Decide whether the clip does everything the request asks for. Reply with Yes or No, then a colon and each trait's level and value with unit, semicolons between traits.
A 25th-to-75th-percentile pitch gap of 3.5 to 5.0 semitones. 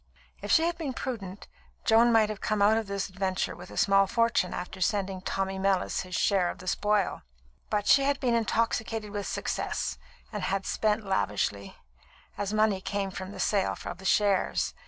No: narrow, 2.6 semitones